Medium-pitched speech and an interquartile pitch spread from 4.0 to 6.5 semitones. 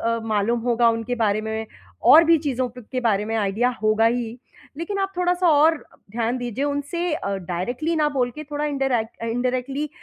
No: high, 245 Hz; average, 4.7 semitones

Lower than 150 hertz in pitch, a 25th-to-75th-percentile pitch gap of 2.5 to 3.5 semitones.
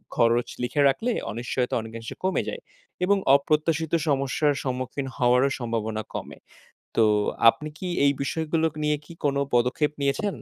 No: medium, 140 Hz; average, 3.9 semitones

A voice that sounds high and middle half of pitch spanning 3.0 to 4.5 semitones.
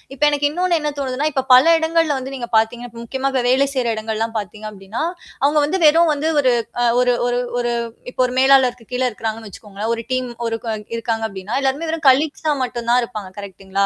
Yes: very high, 250 Hz; average, 4.1 semitones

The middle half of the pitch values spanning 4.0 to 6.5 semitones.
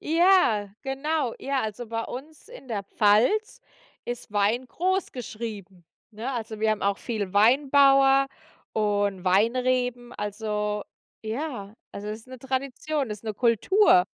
Yes: average, 4.4 semitones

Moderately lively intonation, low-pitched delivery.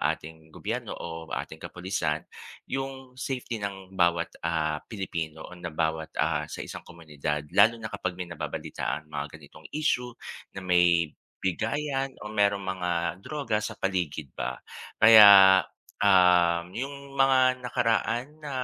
No: wide, 6.0 semitones; very low, 95 Hz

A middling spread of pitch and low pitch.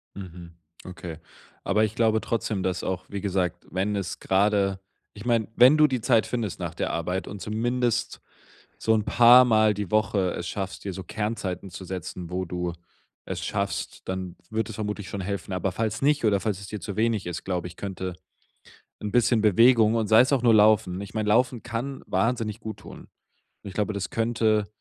Yes: average, 3.2 semitones; low, 105 Hz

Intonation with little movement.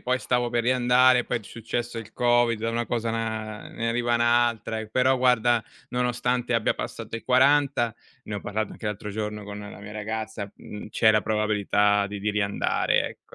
Yes: narrow, 2.3 semitones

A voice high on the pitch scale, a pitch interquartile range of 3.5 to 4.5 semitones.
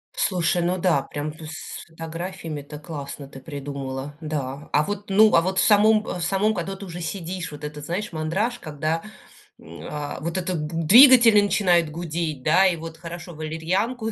No: medium, 165 Hz; average, 3.9 semitones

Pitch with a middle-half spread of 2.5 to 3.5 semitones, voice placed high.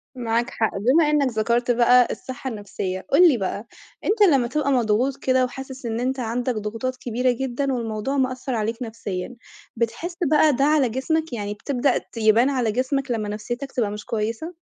Yes: average, 3.2 semitones; high, 245 Hz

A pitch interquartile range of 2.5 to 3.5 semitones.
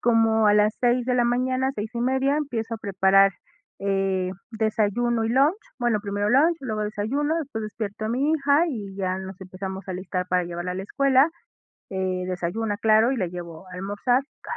No: average, 4.7 semitones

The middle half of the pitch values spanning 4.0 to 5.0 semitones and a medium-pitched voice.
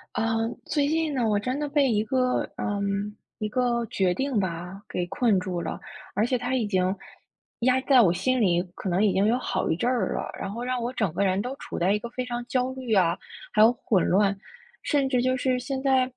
No: average, 4.6 semitones; high, 235 Hz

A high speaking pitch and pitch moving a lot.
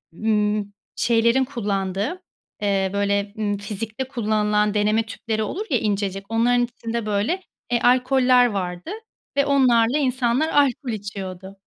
No: high, 220 Hz; average, 3.4 semitones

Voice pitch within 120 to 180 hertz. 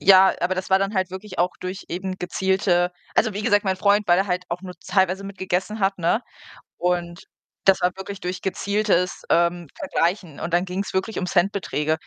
No: high, 190 Hz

